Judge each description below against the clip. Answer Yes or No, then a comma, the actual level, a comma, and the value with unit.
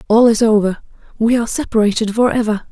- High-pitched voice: Yes, high, 220 Hz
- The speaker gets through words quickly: No, average, 155 wpm